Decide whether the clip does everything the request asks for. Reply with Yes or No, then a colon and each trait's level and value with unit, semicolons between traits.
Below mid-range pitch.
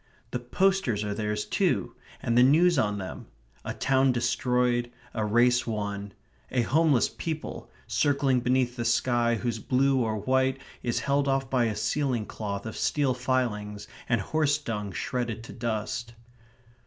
Yes: low, 120 Hz